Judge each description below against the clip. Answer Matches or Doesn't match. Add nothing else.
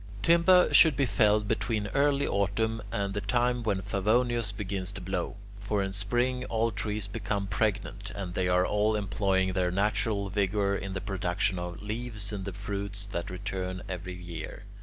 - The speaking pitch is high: Doesn't match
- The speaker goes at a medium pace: Matches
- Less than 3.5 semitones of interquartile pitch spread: Matches